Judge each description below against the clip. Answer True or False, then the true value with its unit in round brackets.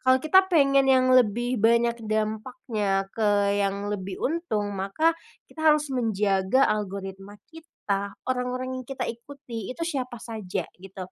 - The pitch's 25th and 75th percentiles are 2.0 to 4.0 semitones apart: False (4.5 semitones)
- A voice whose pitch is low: False (230 Hz)